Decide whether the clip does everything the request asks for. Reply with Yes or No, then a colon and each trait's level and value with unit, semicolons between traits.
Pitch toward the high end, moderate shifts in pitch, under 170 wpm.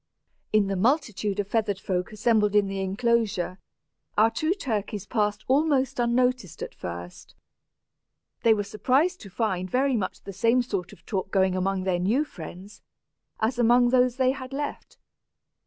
Yes: high, 215 Hz; average, 4.6 semitones; average, 160 wpm